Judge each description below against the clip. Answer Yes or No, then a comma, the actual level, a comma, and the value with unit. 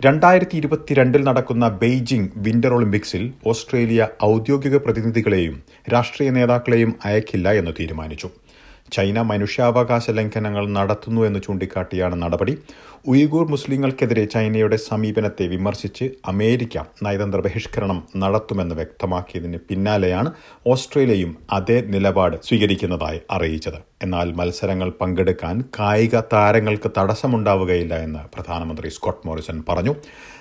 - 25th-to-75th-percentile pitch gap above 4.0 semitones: Yes, average, 4.6 semitones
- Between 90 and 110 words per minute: Yes, average, 95 wpm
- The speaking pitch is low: Yes, low, 105 Hz